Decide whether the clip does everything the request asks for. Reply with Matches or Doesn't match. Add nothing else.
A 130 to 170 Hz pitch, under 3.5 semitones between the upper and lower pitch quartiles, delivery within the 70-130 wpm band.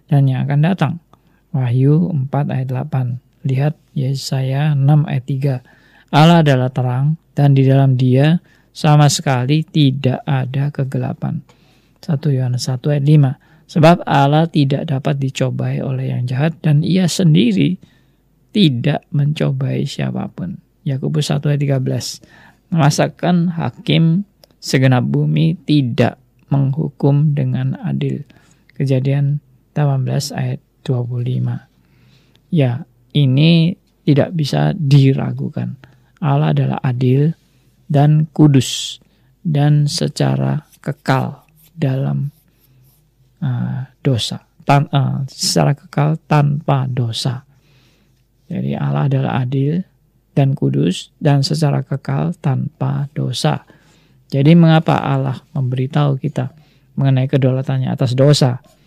Matches